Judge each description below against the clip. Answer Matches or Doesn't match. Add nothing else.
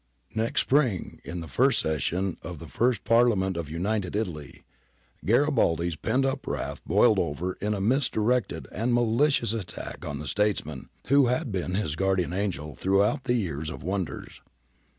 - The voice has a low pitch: Matches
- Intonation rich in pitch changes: Matches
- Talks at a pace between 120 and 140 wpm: Doesn't match